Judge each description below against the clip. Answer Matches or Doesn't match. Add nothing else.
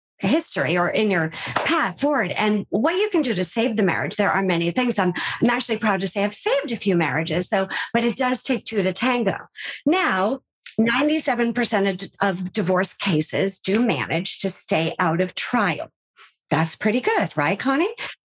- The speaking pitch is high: Matches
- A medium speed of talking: Matches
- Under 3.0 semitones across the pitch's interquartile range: Doesn't match